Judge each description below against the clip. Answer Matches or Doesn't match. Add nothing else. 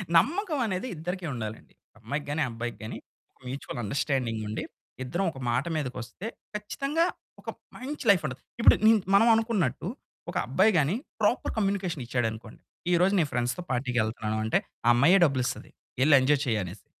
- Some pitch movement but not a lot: Doesn't match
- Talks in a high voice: Doesn't match